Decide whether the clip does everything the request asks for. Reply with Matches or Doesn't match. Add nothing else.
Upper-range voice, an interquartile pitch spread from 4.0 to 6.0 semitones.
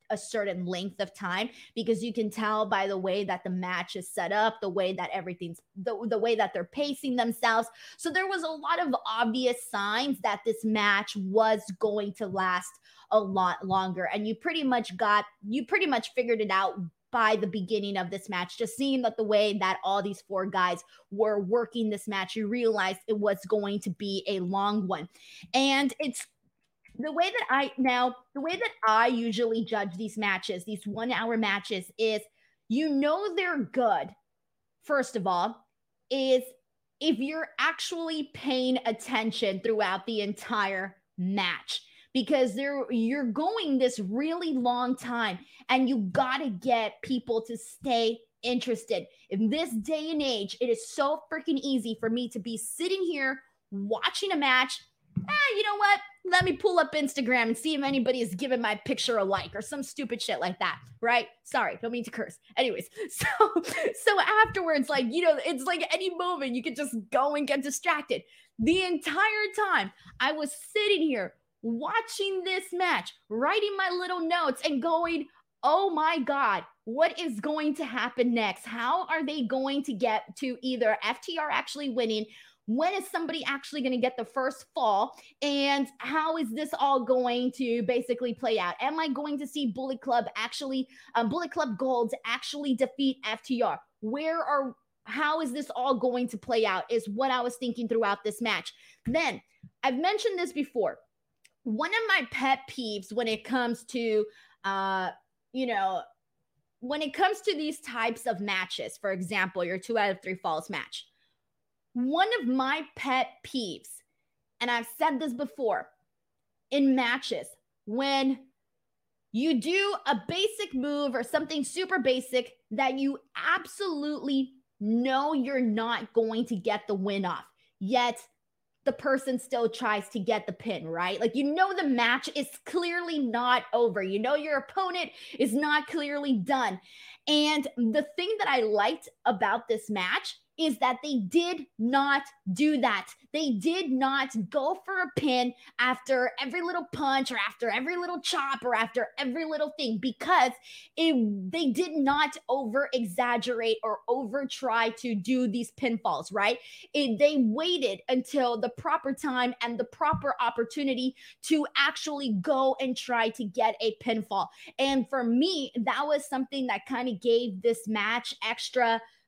Matches